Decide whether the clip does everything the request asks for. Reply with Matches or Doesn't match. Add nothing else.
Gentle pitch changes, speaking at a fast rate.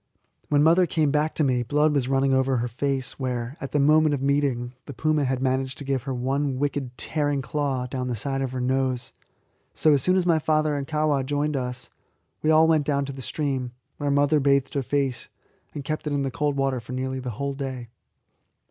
Matches